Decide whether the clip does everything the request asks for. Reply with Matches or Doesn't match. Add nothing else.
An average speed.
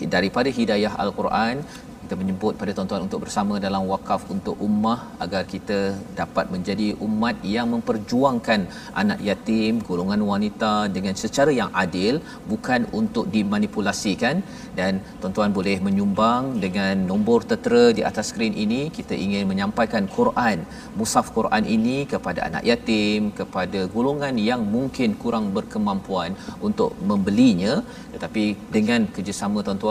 Doesn't match